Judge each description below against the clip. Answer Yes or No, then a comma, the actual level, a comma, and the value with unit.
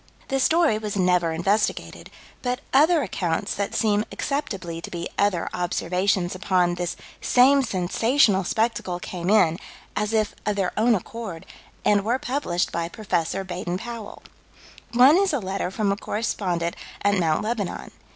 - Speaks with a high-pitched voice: Yes, high, 200 Hz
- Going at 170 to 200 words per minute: No, average, 150 wpm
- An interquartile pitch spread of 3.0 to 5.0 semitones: Yes, average, 4.5 semitones